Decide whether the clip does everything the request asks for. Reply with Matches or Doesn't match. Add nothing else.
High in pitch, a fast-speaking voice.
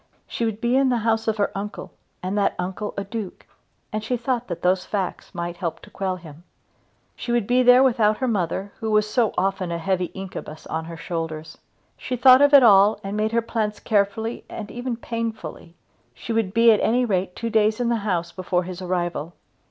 Matches